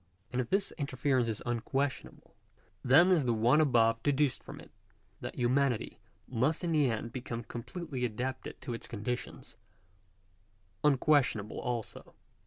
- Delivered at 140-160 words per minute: Yes, average, 145 wpm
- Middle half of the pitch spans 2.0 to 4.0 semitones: Yes, average, 3.6 semitones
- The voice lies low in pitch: Yes, low, 125 Hz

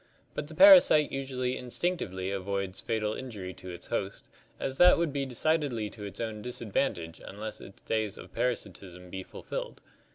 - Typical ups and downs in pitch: No, wide, 5.7 semitones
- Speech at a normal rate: Yes, average, 165 wpm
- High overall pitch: No, low, 110 Hz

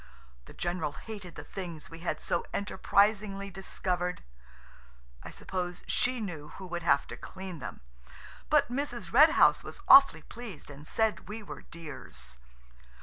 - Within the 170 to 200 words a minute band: No, average, 145 wpm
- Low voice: No, medium, 185 Hz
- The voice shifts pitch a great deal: No, average, 4.4 semitones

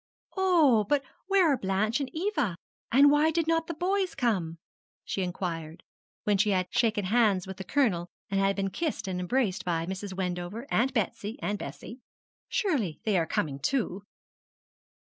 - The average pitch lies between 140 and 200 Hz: No, high, 210 Hz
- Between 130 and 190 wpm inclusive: Yes, average, 165 wpm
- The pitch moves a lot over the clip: Yes, wide, 7.4 semitones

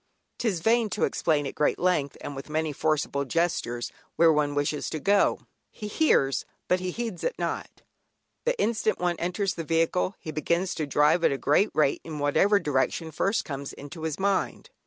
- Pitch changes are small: No, average, 4.6 semitones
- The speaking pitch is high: No, medium, 165 Hz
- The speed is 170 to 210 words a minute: Yes, average, 180 wpm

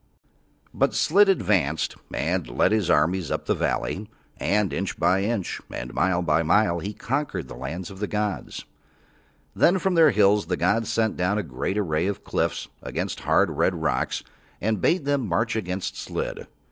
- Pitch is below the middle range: Yes, low, 100 Hz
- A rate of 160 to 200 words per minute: Yes, average, 170 wpm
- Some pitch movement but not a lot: Yes, average, 4.2 semitones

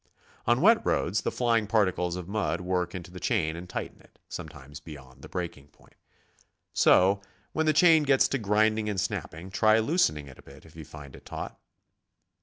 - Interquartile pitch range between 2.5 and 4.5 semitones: No, wide, 5.6 semitones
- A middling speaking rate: Yes, average, 190 wpm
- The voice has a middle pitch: No, very low, 95 Hz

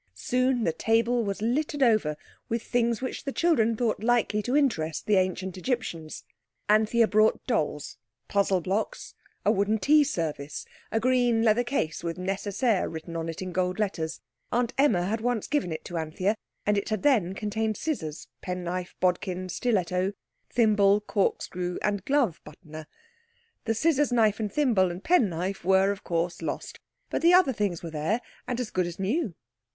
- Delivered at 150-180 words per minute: Yes, average, 165 wpm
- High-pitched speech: Yes, high, 205 Hz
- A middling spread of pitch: Yes, average, 4.9 semitones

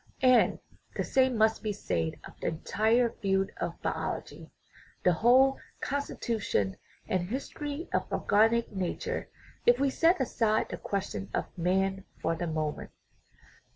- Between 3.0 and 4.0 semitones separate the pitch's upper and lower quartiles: No, wide, 5.4 semitones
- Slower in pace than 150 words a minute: Yes, average, 140 wpm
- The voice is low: No, high, 215 Hz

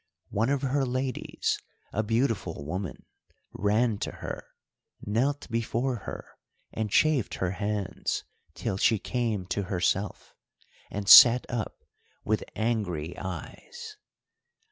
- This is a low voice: Yes, low, 110 Hz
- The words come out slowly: Yes, slow, 115 wpm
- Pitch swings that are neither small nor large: Yes, average, 4.1 semitones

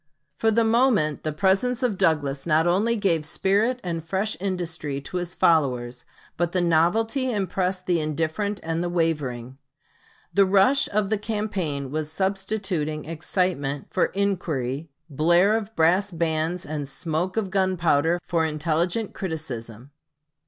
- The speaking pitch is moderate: Yes, medium, 175 Hz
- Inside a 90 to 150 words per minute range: Yes, average, 140 wpm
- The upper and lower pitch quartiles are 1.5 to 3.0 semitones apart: No, average, 4.3 semitones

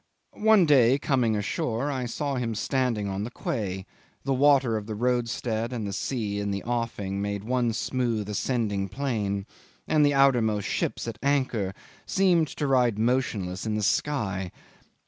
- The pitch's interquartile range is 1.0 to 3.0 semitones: No, average, 4.4 semitones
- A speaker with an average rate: Yes, average, 160 wpm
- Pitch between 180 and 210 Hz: No, low, 115 Hz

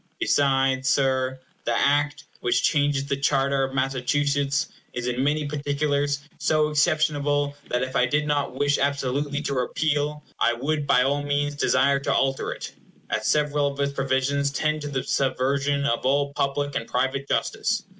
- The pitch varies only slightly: Yes, narrow, 1.4 semitones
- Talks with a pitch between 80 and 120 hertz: No, medium, 140 Hz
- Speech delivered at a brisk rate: No, average, 165 wpm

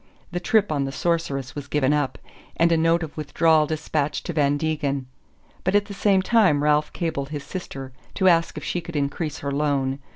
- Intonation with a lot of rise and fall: No, average, 3.0 semitones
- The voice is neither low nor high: Yes, medium, 150 Hz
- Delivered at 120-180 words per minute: No, average, 200 wpm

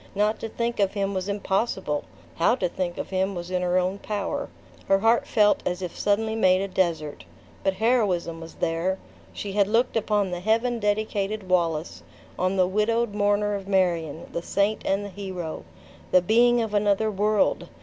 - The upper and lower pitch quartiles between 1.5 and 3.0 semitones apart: Yes, average, 2.7 semitones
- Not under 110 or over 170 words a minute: No, average, 180 wpm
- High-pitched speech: Yes, high, 195 Hz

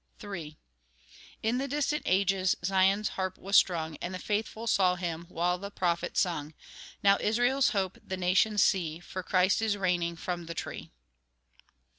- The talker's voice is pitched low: No, medium, 185 Hz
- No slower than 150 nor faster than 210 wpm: Yes, average, 155 wpm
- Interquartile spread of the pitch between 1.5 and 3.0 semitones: Yes, average, 2.7 semitones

